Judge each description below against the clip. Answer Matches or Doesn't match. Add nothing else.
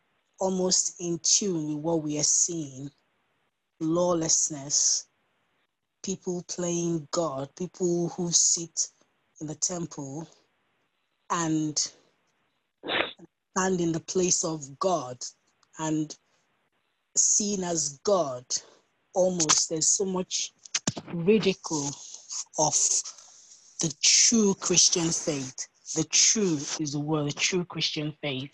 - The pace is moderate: Doesn't match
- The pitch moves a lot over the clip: Doesn't match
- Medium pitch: Matches